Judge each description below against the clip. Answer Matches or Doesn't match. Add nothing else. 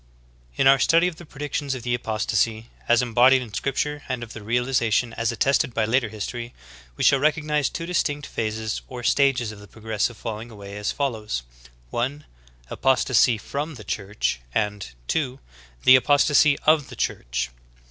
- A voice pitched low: Matches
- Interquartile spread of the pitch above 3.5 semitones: Matches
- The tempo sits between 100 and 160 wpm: Doesn't match